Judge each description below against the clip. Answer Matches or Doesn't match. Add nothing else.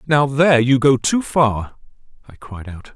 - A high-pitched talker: Doesn't match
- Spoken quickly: Doesn't match